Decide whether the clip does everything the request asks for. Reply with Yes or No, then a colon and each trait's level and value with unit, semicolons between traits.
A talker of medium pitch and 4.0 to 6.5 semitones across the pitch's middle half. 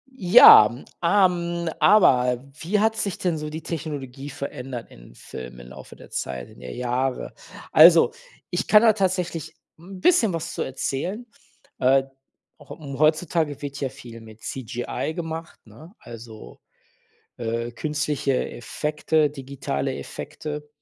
Yes: medium, 150 Hz; wide, 5.5 semitones